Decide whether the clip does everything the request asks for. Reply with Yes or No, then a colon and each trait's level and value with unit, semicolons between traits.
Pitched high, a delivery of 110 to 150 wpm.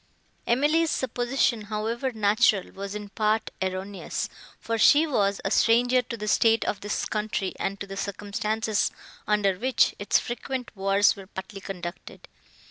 Yes: high, 210 Hz; average, 145 wpm